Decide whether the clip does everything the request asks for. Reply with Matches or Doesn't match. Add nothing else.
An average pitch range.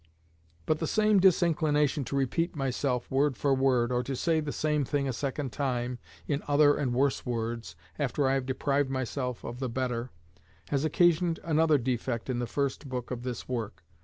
Matches